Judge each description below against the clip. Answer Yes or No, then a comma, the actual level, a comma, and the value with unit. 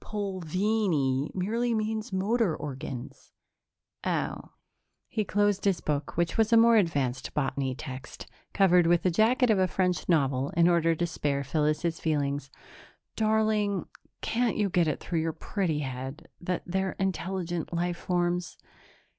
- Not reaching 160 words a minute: Yes, average, 140 wpm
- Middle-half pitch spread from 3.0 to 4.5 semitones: No, average, 5.3 semitones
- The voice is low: No, medium, 175 Hz